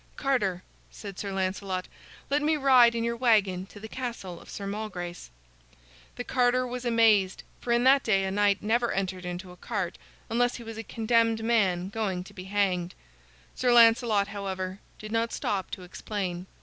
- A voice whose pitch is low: No, high, 210 Hz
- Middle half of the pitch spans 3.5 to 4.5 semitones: Yes, average, 3.8 semitones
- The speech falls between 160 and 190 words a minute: Yes, average, 175 wpm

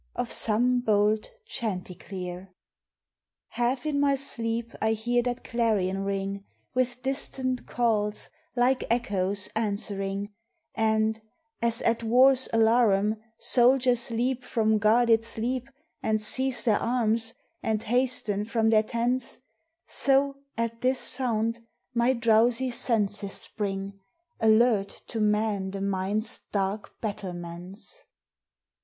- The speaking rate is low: Yes, slow, 110 wpm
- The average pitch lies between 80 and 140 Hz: No, high, 225 Hz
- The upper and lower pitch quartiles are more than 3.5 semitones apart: No, average, 2.9 semitones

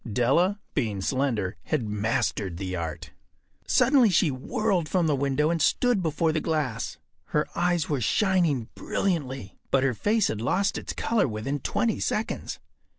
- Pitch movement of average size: No, wide, 7.8 semitones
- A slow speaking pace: No, average, 150 wpm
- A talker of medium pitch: Yes, medium, 145 Hz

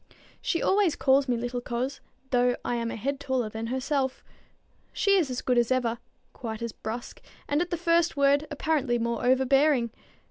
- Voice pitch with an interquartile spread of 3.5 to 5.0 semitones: No, average, 3.1 semitones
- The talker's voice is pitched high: Yes, very high, 260 Hz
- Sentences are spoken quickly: No, average, 180 wpm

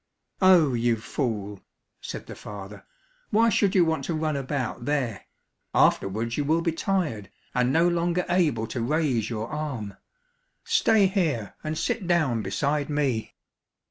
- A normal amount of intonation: No, wide, 6.6 semitones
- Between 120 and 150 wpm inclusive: Yes, average, 145 wpm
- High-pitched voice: No, medium, 145 Hz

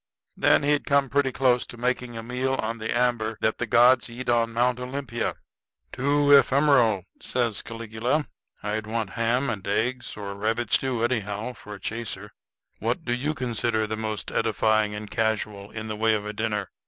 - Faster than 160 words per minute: Yes, average, 180 wpm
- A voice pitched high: No, low, 115 Hz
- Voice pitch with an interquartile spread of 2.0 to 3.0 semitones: Yes, narrow, 2.6 semitones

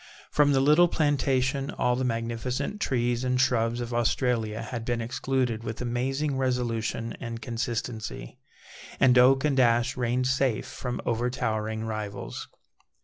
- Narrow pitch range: Yes, narrow, 2.2 semitones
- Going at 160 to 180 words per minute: No, slow, 135 wpm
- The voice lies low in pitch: Yes, low, 125 Hz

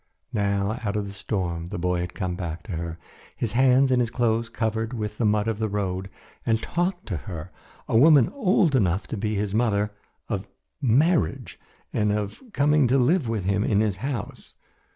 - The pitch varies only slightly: No, average, 3.7 semitones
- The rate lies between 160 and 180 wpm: No, average, 195 wpm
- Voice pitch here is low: Yes, low, 105 Hz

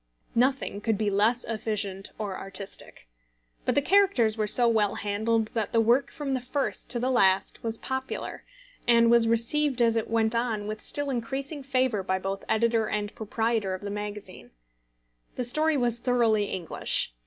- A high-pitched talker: Yes, high, 230 Hz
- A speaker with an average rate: Yes, average, 170 wpm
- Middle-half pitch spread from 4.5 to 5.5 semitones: No, average, 3.1 semitones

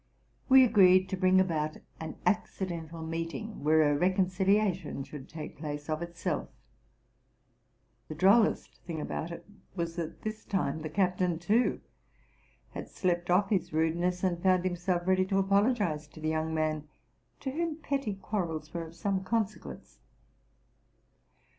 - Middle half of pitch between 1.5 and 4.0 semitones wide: Yes, average, 3.4 semitones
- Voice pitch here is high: No, medium, 180 Hz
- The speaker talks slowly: No, average, 145 wpm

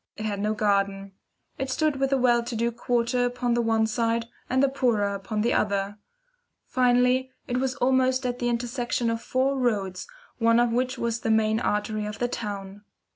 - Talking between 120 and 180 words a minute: No, average, 190 wpm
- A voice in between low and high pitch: No, high, 235 Hz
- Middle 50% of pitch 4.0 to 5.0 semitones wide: No, average, 2.8 semitones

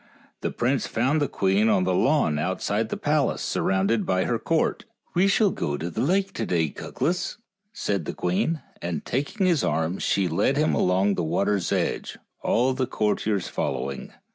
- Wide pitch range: Yes, wide, 7.9 semitones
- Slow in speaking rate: No, average, 180 wpm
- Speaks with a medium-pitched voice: No, low, 105 Hz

